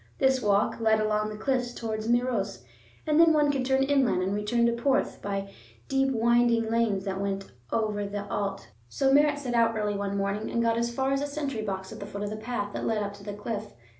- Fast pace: Yes, fast, 230 wpm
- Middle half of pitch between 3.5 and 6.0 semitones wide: Yes, average, 3.9 semitones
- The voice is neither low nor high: No, high, 225 Hz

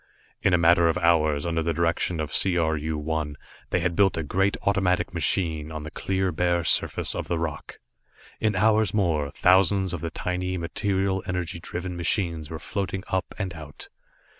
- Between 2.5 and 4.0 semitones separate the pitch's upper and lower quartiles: Yes, average, 2.8 semitones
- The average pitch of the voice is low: Yes, very low, 85 Hz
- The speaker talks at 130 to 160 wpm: No, average, 185 wpm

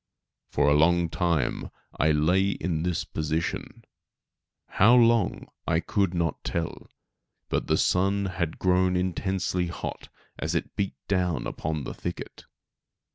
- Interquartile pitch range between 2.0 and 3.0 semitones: Yes, average, 2.7 semitones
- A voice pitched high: No, very low, 90 Hz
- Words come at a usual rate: No, slow, 130 wpm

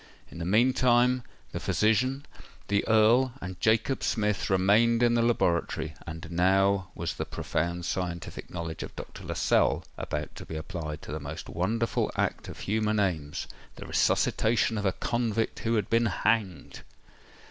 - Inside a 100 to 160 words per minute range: Yes, average, 150 wpm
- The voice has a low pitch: Yes, low, 105 Hz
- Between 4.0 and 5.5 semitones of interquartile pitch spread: Yes, average, 5.1 semitones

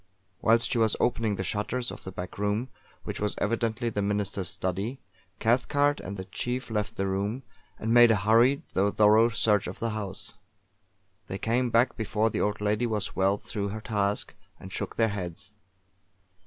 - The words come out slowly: No, average, 180 wpm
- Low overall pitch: Yes, low, 105 Hz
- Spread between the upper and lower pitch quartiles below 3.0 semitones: Yes, narrow, 2.5 semitones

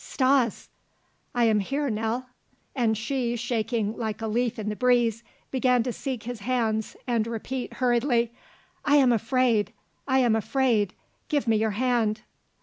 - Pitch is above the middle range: Yes, high, 235 Hz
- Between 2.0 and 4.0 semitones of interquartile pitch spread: Yes, narrow, 2.5 semitones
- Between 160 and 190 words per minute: No, average, 150 wpm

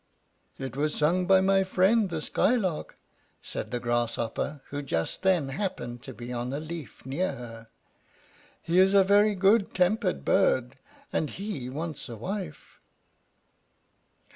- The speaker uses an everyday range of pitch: No, wide, 7.0 semitones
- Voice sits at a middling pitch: Yes, medium, 160 Hz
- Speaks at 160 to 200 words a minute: No, average, 140 wpm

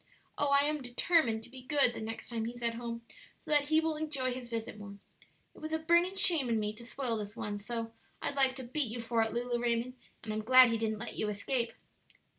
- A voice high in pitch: Yes, high, 240 Hz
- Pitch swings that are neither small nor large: Yes, average, 3.8 semitones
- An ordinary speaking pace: No, fast, 240 wpm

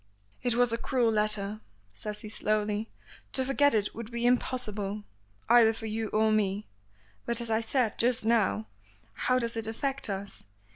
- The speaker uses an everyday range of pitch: No, narrow, 2.2 semitones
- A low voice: No, high, 225 Hz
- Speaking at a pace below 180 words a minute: Yes, average, 165 wpm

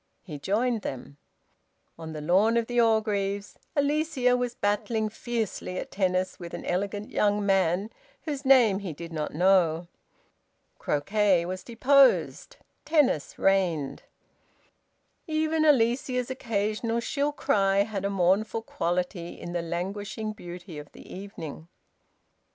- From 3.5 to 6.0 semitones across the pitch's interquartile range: Yes, average, 4.8 semitones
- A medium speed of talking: No, slow, 125 wpm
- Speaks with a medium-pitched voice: No, high, 200 Hz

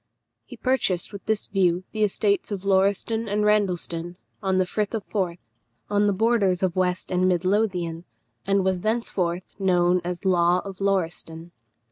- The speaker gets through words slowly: No, average, 160 wpm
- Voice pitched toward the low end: No, high, 190 Hz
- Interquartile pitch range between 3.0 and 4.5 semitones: No, narrow, 2.5 semitones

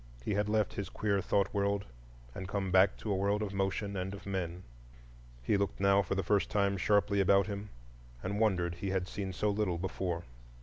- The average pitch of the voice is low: Yes, low, 100 Hz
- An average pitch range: No, narrow, 1.2 semitones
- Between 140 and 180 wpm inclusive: No, fast, 205 wpm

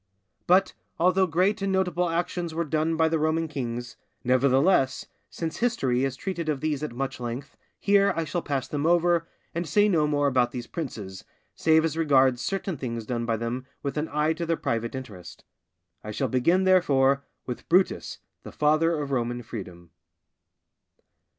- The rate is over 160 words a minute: Yes, average, 170 wpm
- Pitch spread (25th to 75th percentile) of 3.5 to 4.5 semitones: No, average, 4.9 semitones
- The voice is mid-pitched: Yes, medium, 150 Hz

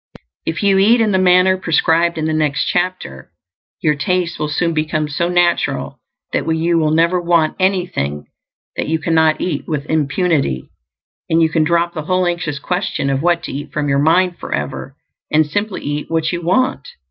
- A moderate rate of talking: Yes, average, 180 wpm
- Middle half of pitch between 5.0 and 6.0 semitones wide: No, average, 2.8 semitones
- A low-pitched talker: No, medium, 165 Hz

